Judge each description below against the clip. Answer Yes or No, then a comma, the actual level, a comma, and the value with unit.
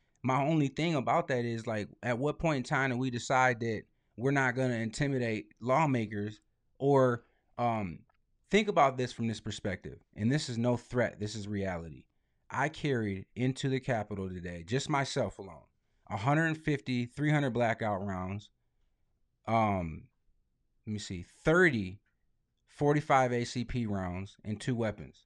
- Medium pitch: No, low, 120 Hz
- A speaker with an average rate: Yes, average, 145 wpm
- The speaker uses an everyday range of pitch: Yes, average, 4.5 semitones